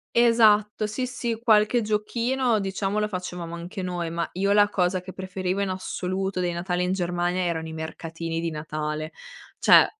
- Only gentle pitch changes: No, average, 3.5 semitones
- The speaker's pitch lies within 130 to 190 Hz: Yes, medium, 185 Hz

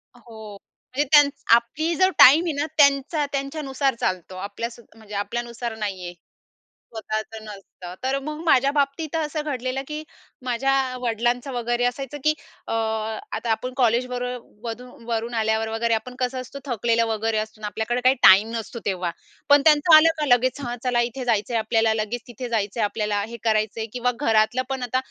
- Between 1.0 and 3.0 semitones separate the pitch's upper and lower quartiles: No, average, 3.5 semitones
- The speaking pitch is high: Yes, high, 240 Hz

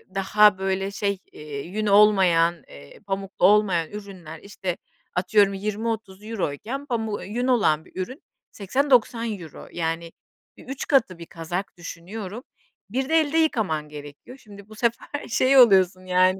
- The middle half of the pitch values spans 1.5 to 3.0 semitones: No, average, 4.0 semitones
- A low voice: No, high, 200 Hz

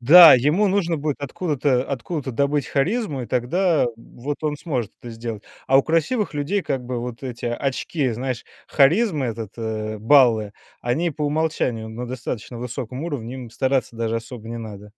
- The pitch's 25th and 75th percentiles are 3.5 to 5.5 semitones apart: Yes, average, 4.3 semitones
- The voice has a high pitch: No, low, 130 Hz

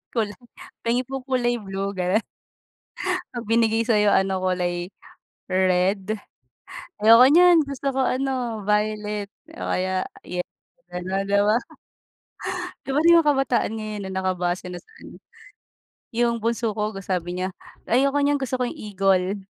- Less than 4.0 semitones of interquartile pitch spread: No, average, 4.3 semitones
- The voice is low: No, high, 210 Hz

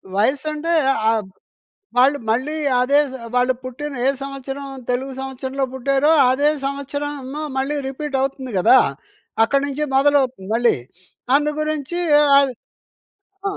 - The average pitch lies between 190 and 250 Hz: No, very high, 275 Hz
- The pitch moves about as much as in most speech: No, narrow, 2.0 semitones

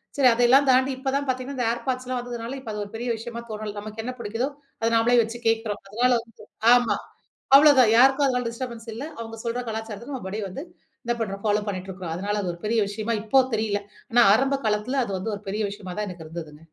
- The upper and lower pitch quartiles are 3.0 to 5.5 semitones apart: Yes, average, 3.3 semitones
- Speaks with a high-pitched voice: Yes, high, 230 Hz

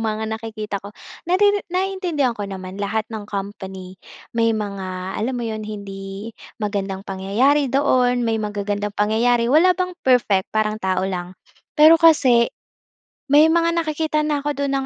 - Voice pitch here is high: Yes, high, 220 Hz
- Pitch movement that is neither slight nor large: No, wide, 6.2 semitones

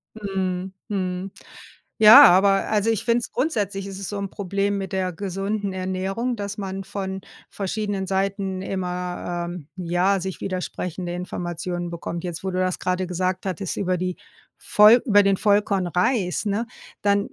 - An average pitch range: No, narrow, 1.8 semitones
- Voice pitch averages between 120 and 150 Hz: No, high, 190 Hz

